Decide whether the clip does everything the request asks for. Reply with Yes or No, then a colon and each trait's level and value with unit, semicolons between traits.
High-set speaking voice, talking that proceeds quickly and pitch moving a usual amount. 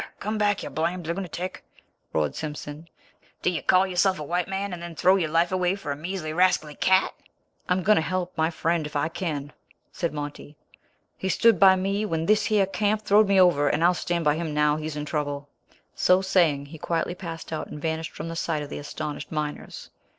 No: medium, 170 Hz; fast, 210 wpm; average, 3.6 semitones